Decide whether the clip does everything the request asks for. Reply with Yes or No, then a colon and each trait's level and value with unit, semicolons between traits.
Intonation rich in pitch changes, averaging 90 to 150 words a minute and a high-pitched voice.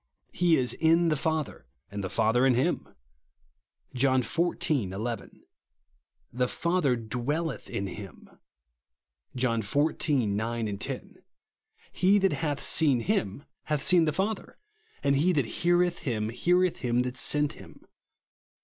No: wide, 6.1 semitones; average, 140 wpm; low, 135 Hz